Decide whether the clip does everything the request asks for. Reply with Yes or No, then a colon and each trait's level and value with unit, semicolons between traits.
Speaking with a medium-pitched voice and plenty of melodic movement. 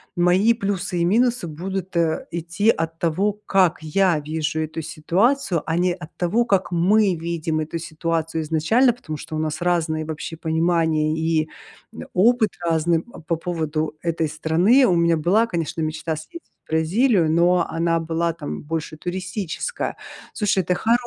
No: medium, 170 Hz; average, 3.0 semitones